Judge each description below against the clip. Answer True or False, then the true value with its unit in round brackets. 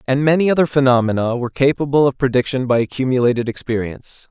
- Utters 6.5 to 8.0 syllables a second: True (6.7 syllables/s)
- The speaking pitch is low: True (130 Hz)